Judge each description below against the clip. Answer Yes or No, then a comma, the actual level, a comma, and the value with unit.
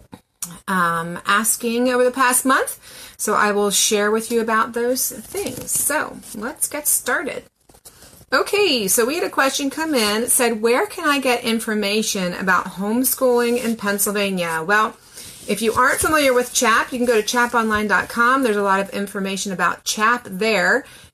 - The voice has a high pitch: Yes, high, 230 Hz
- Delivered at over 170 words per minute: No, average, 165 wpm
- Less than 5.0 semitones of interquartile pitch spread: Yes, average, 3.5 semitones